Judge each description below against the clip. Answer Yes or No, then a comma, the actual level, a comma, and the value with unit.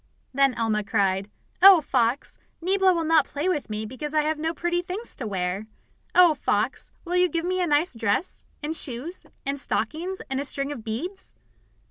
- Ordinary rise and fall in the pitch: No, wide, 7.2 semitones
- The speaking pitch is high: Yes, very high, 295 Hz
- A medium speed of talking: Yes, average, 185 wpm